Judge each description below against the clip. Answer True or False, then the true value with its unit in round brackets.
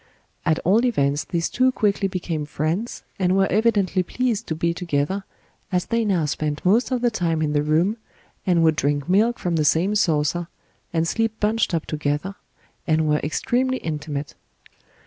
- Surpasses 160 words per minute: True (170 wpm)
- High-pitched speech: False (175 Hz)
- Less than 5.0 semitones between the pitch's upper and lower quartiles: False (5.4 semitones)